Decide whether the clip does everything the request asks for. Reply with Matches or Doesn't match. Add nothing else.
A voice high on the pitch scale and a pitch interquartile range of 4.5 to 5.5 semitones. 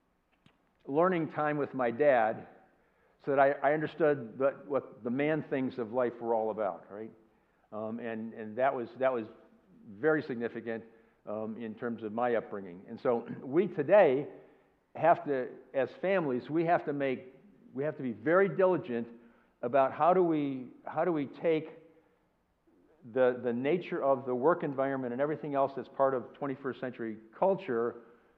Doesn't match